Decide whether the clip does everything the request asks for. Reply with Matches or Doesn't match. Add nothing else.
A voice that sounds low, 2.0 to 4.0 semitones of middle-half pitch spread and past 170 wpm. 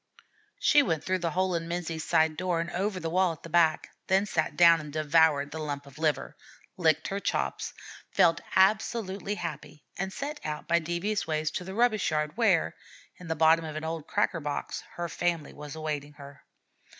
Doesn't match